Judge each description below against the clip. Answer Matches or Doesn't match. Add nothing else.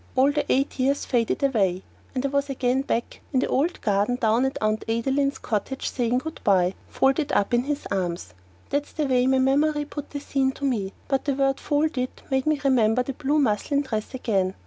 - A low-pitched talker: Doesn't match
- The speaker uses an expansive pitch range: Doesn't match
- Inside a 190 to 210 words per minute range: Matches